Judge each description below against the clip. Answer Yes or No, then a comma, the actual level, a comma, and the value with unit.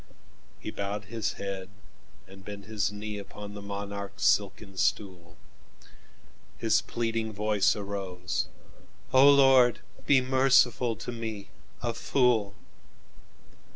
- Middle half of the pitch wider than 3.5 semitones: No, average, 2.8 semitones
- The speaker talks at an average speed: No, slow, 95 wpm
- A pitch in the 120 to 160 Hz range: No, low, 105 Hz